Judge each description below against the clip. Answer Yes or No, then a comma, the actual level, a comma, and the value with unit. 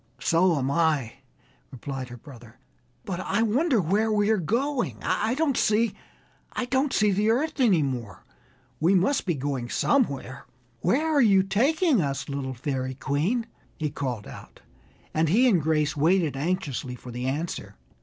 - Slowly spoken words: No, average, 150 wpm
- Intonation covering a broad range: Yes, wide, 8.4 semitones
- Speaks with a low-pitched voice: No, medium, 170 Hz